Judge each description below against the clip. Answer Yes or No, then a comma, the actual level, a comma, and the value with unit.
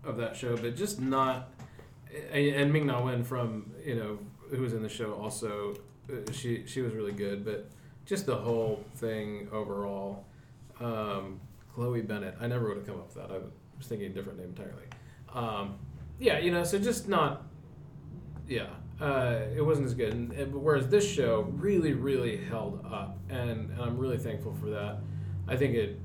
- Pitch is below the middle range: Yes, low, 120 Hz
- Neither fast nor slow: Yes, average, 185 wpm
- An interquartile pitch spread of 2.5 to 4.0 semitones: No, average, 4.6 semitones